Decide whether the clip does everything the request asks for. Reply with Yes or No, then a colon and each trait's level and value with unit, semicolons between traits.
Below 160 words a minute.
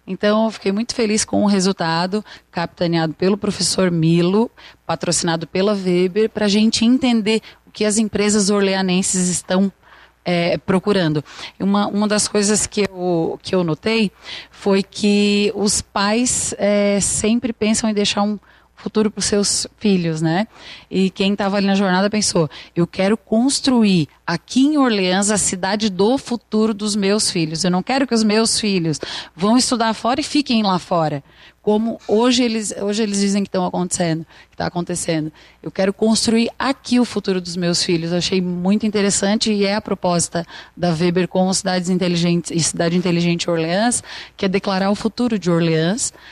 No: average, 170 wpm